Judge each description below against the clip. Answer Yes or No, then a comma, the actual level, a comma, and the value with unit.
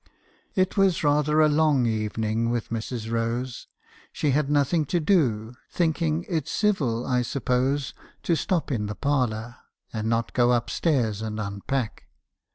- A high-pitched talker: No, low, 125 Hz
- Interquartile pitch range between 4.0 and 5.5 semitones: Yes, average, 4.9 semitones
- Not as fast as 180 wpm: Yes, average, 150 wpm